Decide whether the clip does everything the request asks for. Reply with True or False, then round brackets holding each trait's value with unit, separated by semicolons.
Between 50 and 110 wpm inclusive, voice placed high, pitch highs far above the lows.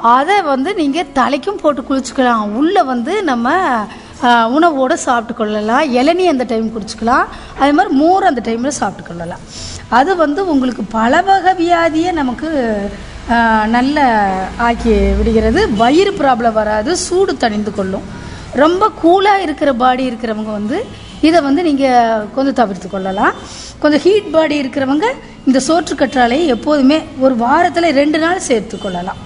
False (130 wpm; 265 Hz; 6.4 semitones)